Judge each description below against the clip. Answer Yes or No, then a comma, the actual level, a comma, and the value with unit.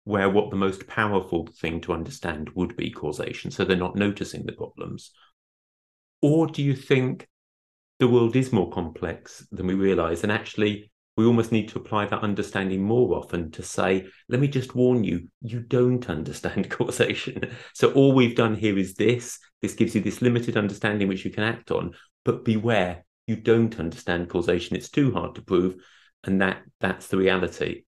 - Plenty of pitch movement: No, average, 4.2 semitones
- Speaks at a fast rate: No, average, 185 wpm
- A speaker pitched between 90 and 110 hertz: Yes, low, 105 Hz